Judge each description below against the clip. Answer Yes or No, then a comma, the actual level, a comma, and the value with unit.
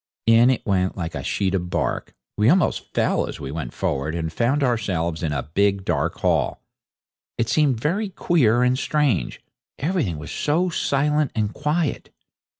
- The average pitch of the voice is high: No, low, 115 Hz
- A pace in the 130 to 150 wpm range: No, average, 165 wpm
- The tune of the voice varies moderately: No, wide, 8.6 semitones